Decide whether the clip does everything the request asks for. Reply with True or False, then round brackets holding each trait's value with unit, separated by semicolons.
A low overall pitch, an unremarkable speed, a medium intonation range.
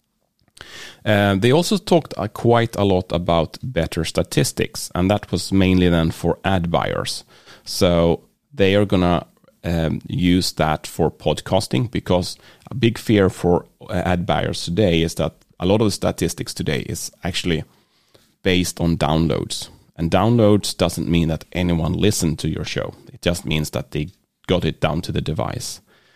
True (90 Hz; 160 wpm; 3.4 semitones)